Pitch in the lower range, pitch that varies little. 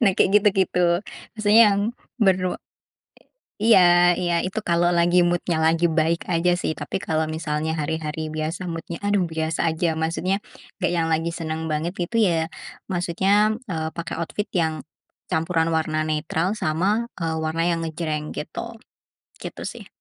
No: medium, 170 Hz; narrow, 2.1 semitones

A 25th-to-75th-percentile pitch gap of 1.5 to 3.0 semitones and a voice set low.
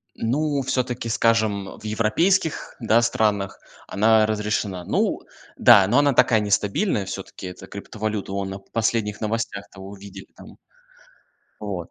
Yes: narrow, 2.5 semitones; low, 110 Hz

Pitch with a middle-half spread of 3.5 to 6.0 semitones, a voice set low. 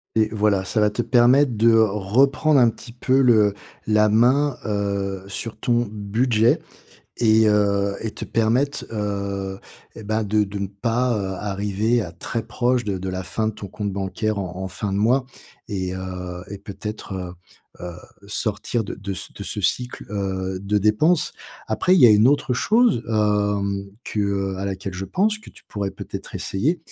No: average, 3.0 semitones; low, 105 Hz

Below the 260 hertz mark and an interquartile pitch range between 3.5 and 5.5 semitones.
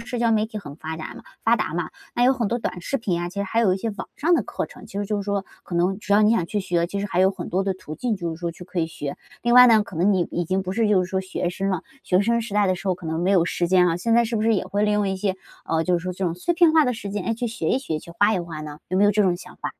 Yes: high, 195 Hz; average, 3.8 semitones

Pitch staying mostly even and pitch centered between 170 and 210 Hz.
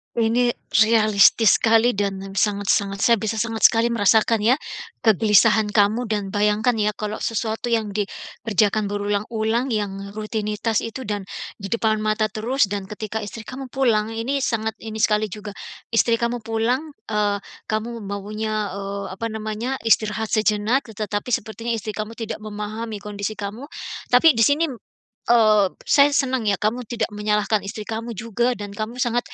No: narrow, 1.8 semitones; high, 220 Hz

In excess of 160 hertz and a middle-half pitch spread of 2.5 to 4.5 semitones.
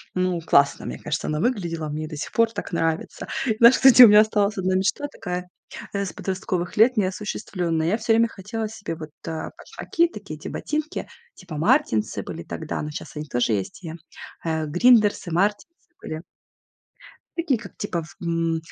No: medium, 185 Hz; wide, 5.4 semitones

